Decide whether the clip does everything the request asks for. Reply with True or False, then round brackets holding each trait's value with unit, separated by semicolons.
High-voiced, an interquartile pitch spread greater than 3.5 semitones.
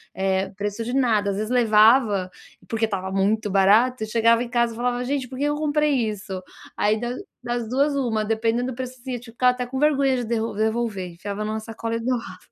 False (230 Hz; 2.9 semitones)